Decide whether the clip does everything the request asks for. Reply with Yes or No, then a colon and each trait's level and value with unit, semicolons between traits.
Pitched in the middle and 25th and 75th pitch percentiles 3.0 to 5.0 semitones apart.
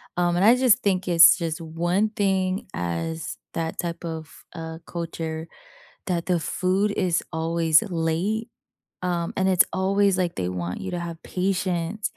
No: medium, 175 Hz; narrow, 2.6 semitones